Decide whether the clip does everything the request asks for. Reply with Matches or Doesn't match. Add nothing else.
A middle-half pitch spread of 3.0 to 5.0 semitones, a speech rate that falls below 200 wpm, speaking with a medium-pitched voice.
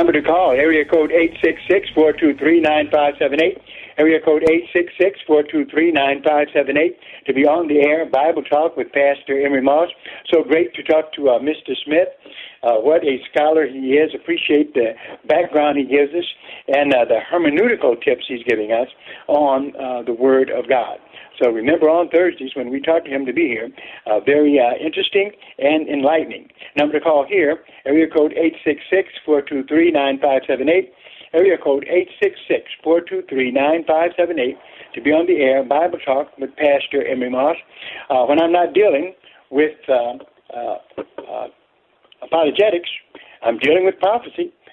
Matches